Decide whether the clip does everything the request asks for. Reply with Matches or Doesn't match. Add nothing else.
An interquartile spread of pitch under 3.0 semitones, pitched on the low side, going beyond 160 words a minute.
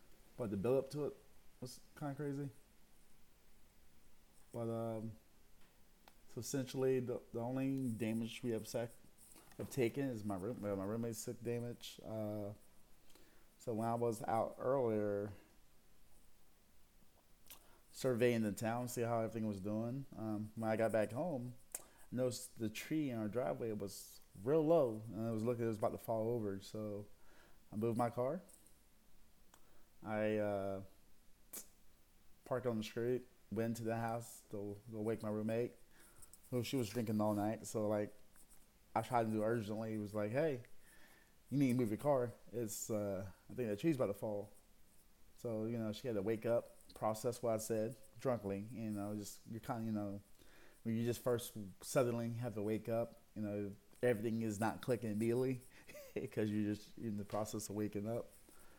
Matches